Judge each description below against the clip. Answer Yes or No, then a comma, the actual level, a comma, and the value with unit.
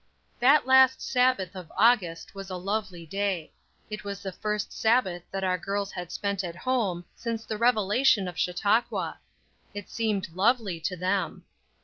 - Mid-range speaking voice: No, high, 200 Hz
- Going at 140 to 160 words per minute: Yes, average, 155 wpm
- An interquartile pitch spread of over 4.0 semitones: No, average, 3.6 semitones